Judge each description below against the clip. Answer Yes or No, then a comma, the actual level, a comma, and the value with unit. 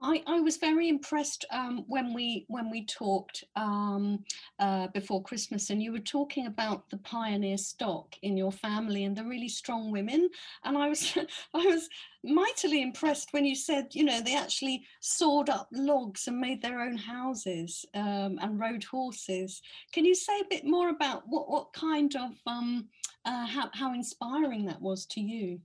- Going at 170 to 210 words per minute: Yes, average, 180 wpm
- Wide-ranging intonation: Yes, wide, 6.2 semitones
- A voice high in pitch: Yes, high, 245 Hz